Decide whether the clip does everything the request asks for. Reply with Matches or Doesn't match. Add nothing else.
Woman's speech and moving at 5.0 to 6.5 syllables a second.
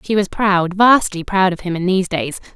Matches